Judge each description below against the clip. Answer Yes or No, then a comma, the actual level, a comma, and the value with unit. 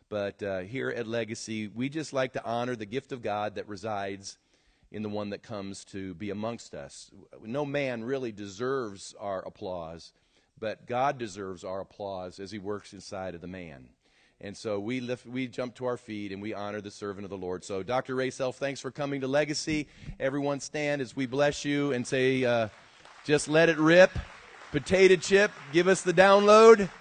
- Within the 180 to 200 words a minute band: Yes, average, 195 wpm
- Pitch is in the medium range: No, low, 120 Hz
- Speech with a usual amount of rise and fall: No, wide, 5.8 semitones